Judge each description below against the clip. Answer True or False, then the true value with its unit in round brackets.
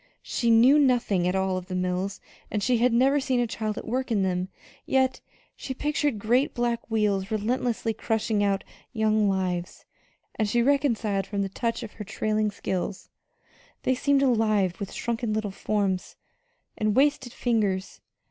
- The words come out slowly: False (165 wpm)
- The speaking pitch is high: True (220 Hz)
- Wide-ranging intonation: False (3.7 semitones)